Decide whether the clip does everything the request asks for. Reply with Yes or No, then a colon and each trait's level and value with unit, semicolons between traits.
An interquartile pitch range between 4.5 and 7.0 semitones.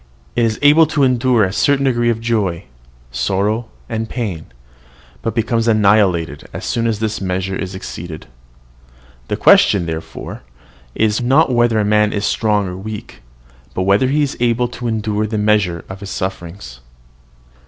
No: average, 3.6 semitones